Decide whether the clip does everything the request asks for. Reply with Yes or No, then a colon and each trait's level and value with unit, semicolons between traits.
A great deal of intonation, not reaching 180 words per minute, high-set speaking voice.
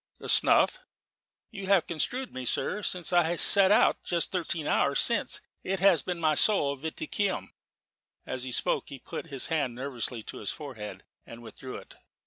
No: wide, 6.1 semitones; average, 170 wpm; medium, 160 Hz